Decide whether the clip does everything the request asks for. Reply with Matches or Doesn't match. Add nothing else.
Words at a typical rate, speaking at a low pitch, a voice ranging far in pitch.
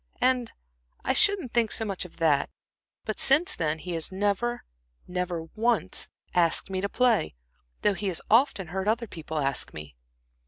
Doesn't match